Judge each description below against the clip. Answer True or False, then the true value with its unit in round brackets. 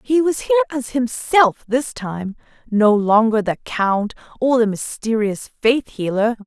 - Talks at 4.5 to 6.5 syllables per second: False (4.2 syllables/s)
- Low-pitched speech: False (235 Hz)